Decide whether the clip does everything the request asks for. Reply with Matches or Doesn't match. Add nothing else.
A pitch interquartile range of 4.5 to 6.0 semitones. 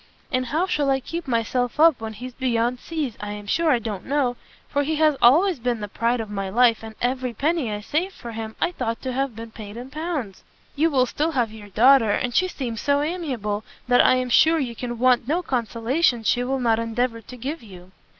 Doesn't match